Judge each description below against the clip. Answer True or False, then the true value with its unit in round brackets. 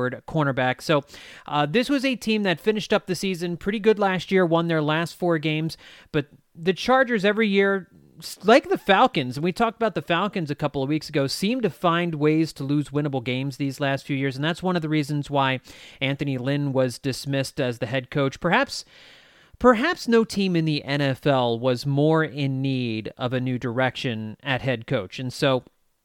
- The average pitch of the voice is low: False (150 Hz)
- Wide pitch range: True (5.7 semitones)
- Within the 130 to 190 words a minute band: False (200 wpm)